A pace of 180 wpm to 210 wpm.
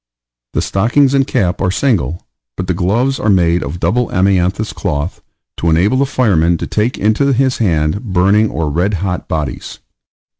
No: average, 165 wpm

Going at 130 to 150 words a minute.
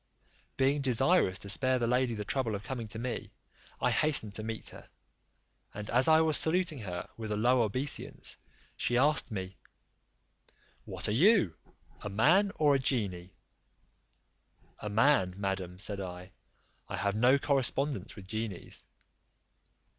Yes: average, 145 wpm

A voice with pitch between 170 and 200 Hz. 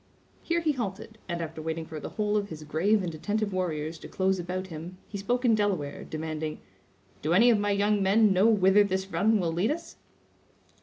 Yes: high, 190 Hz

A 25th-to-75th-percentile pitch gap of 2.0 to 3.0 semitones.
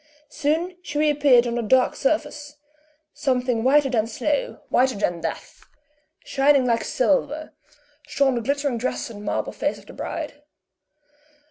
No: average, 3.4 semitones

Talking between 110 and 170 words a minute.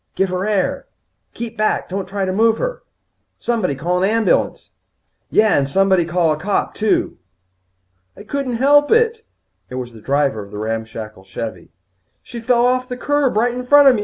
No: average, 185 wpm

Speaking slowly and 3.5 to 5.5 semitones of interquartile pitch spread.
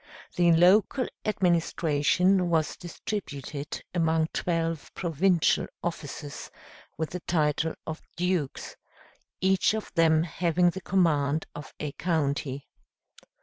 No: slow, 105 wpm; average, 3.0 semitones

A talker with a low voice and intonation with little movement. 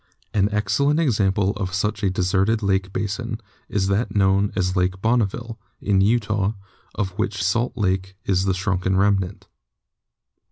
Yes: low, 100 Hz; narrow, 2.2 semitones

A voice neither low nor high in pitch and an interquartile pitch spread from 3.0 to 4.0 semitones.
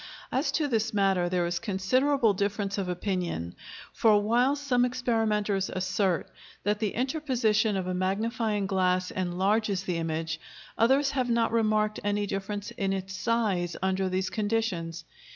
No: high, 205 Hz; average, 3.5 semitones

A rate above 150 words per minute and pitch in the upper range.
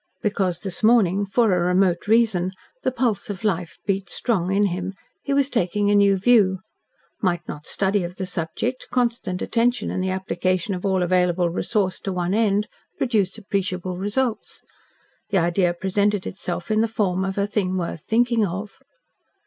Yes: average, 170 wpm; high, 195 Hz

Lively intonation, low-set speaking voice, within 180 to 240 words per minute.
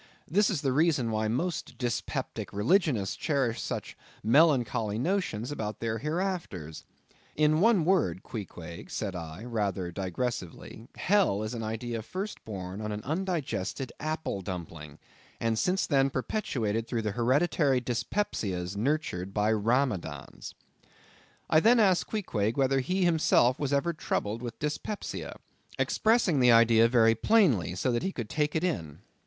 No: wide, 6.9 semitones; low, 120 Hz; average, 140 wpm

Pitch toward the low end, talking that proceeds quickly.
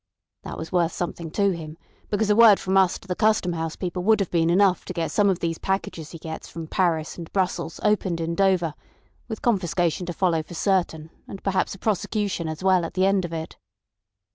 No: medium, 180 Hz; fast, 215 wpm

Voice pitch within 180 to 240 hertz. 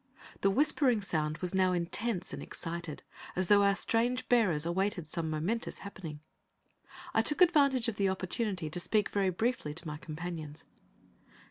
Yes: high, 190 Hz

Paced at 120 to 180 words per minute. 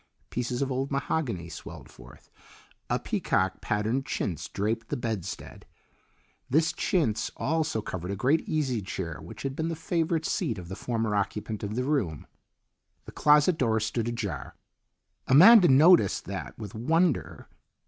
Yes: average, 150 wpm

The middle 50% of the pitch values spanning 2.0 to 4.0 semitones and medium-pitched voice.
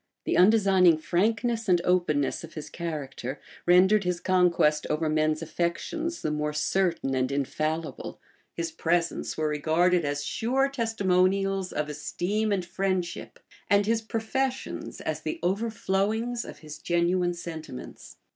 No: average, 4.6 semitones; medium, 180 Hz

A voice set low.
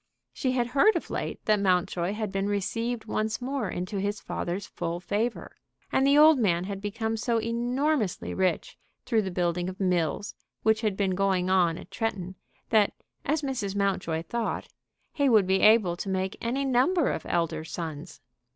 No: high, 205 Hz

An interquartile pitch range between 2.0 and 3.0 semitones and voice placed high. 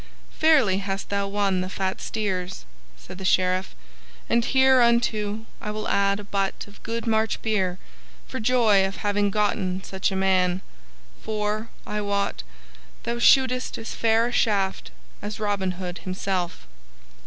Yes: narrow, 2.5 semitones; high, 205 Hz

